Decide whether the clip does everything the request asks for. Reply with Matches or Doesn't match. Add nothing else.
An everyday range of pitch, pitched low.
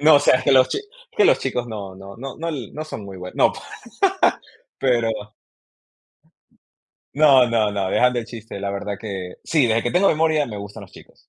Doesn't match